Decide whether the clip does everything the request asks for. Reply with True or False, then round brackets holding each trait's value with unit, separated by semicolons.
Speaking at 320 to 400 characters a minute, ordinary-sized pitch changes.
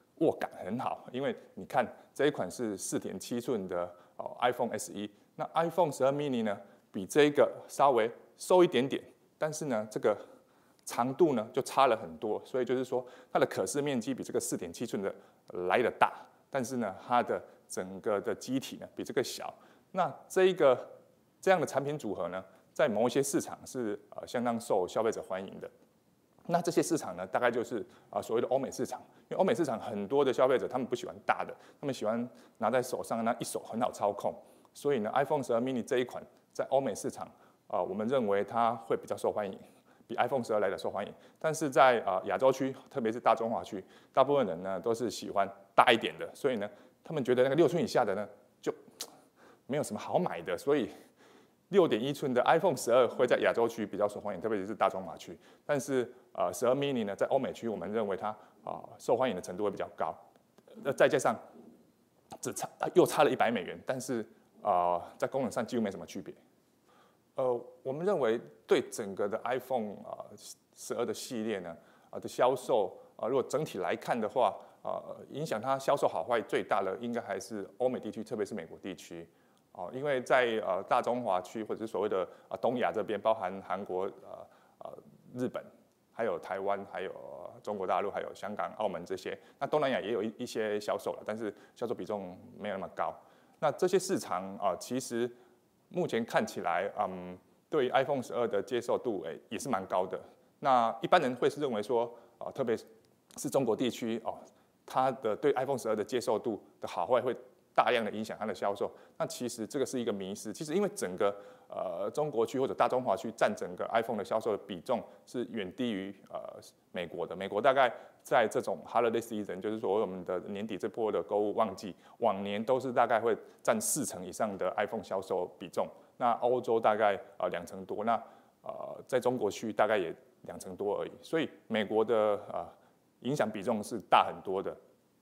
False (325 characters per minute; 5.9 semitones)